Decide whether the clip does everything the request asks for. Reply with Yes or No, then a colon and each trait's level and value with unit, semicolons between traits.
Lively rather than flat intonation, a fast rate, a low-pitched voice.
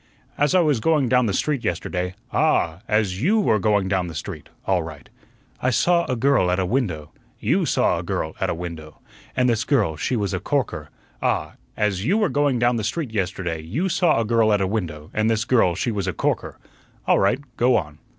Yes: wide, 6.2 semitones; fast, 230 wpm; low, 110 Hz